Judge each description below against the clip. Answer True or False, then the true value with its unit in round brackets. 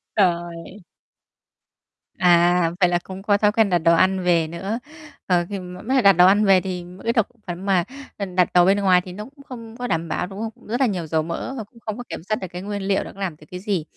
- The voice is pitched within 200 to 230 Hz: False (190 Hz)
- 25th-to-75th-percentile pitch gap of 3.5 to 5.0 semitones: False (2.9 semitones)